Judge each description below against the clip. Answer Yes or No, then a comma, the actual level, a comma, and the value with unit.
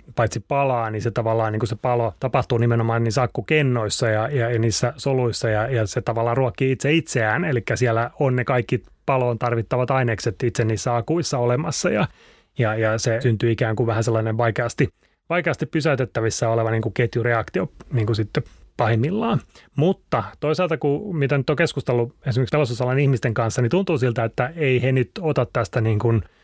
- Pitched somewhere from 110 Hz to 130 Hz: Yes, low, 120 Hz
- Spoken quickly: Yes, fast, 175 wpm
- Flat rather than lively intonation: No, average, 3.2 semitones